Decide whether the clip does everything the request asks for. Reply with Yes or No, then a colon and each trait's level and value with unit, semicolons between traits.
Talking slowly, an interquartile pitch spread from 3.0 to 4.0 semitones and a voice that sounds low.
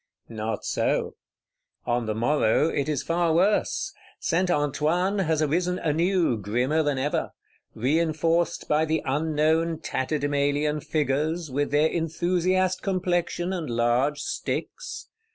No: slow, 115 wpm; average, 3.3 semitones; medium, 155 Hz